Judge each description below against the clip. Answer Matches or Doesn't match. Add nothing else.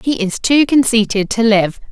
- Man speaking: Doesn't match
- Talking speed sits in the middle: Matches